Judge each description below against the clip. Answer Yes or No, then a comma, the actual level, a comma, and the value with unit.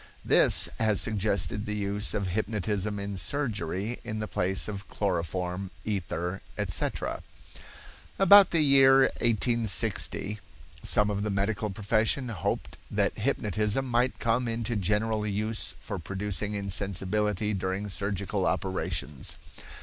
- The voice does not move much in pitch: Yes, narrow, 2.3 semitones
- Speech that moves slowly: Yes, slow, 120 wpm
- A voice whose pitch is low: Yes, low, 105 Hz